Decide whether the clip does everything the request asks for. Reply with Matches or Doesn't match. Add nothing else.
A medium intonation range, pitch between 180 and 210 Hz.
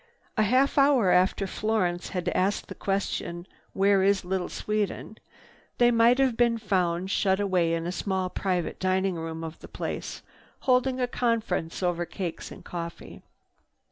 Matches